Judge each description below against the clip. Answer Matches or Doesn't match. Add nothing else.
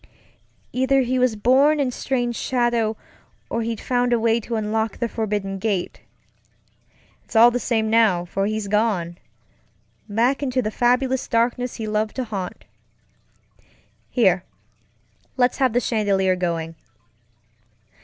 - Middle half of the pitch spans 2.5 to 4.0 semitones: Matches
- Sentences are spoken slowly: Matches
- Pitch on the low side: Doesn't match